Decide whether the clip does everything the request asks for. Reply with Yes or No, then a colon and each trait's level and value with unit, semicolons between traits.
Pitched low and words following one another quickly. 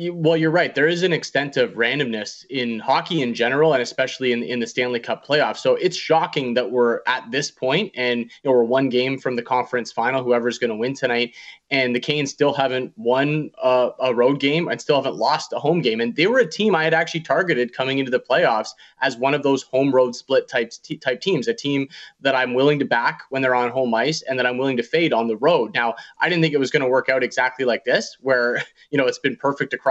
Yes: low, 130 Hz; fast, 255 wpm